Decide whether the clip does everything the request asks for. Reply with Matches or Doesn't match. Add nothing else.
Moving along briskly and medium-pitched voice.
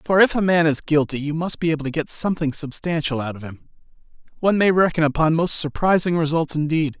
Matches